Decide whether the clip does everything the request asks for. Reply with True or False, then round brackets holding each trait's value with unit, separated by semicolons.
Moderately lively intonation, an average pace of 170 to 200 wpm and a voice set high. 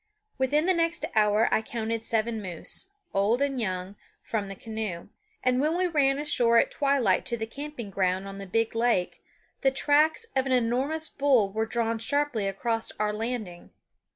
True (4.7 semitones; 175 wpm; 230 Hz)